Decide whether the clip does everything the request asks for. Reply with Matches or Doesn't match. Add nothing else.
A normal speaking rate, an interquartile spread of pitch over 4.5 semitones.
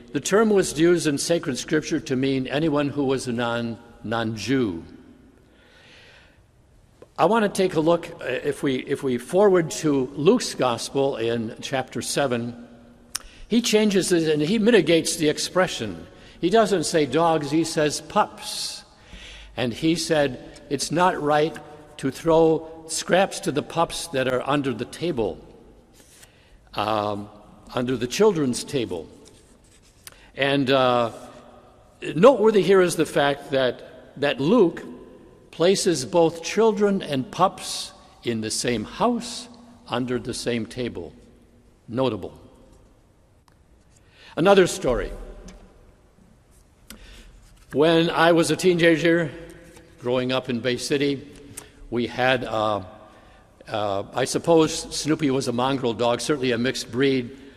Doesn't match